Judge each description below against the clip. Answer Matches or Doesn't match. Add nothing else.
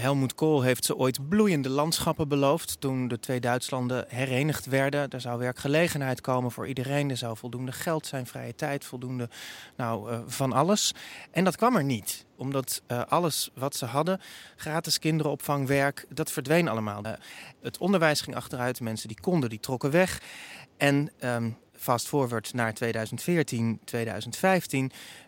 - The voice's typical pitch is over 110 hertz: Matches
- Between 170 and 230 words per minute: Doesn't match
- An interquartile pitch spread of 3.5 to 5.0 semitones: Matches